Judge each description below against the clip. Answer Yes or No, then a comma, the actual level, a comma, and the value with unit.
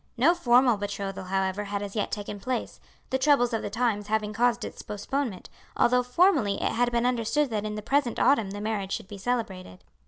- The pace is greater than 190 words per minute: Yes, average, 200 wpm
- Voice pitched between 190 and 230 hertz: Yes, high, 220 Hz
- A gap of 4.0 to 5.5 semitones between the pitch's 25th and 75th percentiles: No, average, 3.5 semitones